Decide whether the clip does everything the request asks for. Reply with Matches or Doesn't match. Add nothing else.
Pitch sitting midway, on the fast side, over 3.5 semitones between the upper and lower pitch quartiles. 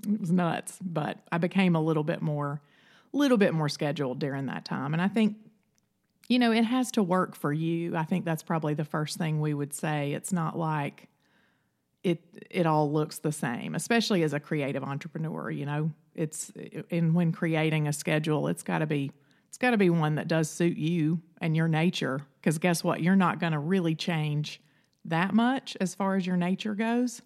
Matches